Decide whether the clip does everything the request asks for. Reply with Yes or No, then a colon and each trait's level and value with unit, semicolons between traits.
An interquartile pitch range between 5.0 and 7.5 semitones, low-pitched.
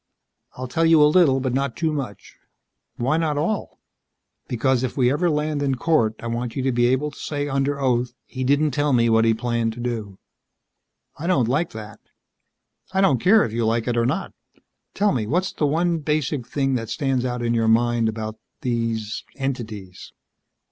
No: average, 4.2 semitones; low, 130 Hz